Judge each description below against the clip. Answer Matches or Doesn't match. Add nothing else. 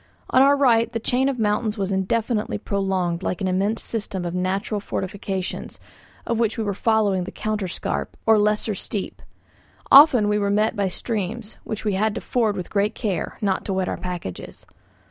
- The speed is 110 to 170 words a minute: Doesn't match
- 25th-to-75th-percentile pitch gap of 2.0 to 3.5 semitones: Matches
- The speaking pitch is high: Matches